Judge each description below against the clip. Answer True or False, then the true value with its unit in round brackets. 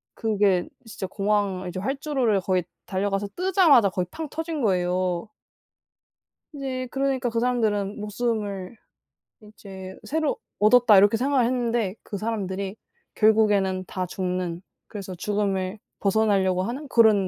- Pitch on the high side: True (210 Hz)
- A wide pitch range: False (4.1 semitones)